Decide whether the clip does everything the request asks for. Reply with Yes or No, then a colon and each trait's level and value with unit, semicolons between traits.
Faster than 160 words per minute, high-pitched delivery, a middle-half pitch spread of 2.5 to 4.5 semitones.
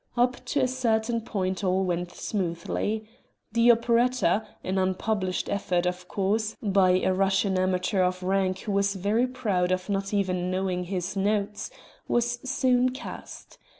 No: average, 150 wpm; high, 195 Hz; average, 3.4 semitones